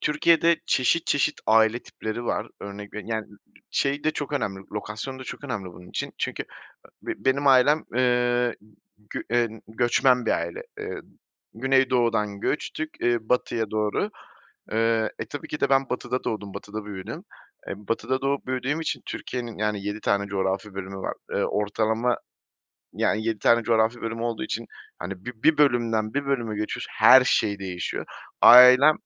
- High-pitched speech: No, low, 115 Hz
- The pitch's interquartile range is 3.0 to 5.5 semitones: Yes, average, 3.6 semitones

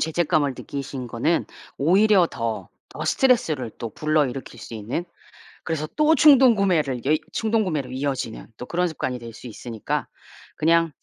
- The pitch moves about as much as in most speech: No, wide, 6.0 semitones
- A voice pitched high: No, medium, 155 Hz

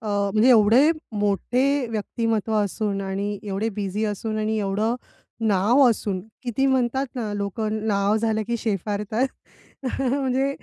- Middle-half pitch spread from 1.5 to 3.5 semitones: Yes, average, 2.8 semitones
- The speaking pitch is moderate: No, high, 215 Hz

